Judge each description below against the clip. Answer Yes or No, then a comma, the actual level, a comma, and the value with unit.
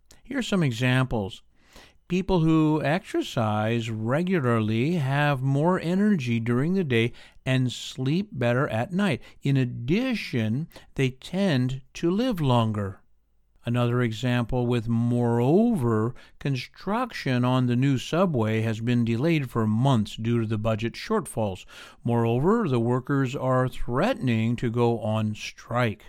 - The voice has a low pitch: Yes, low, 125 Hz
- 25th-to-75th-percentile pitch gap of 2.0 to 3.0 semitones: No, average, 4.8 semitones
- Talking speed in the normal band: No, slow, 125 wpm